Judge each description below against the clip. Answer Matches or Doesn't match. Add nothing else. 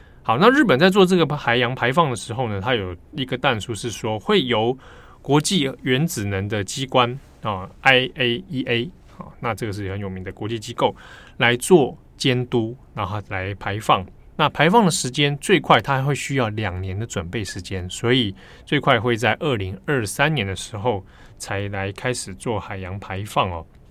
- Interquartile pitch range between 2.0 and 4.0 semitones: Doesn't match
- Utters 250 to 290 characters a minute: Matches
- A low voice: Matches